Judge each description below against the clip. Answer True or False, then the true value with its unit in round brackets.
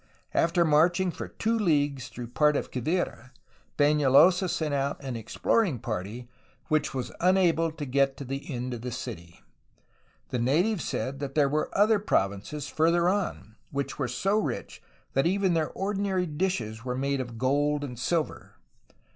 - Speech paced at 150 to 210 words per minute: True (160 wpm)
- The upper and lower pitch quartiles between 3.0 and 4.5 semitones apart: False (5.3 semitones)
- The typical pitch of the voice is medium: True (145 Hz)